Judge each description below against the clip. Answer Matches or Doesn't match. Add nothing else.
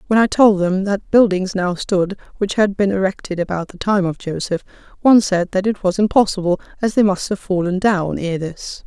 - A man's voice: Doesn't match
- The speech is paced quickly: Matches